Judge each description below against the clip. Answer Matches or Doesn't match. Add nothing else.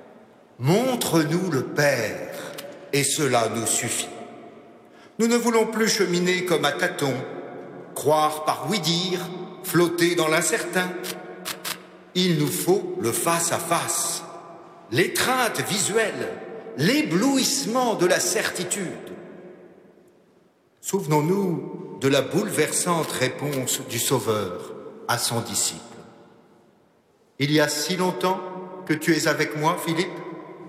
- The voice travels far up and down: Doesn't match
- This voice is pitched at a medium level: Matches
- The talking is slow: Matches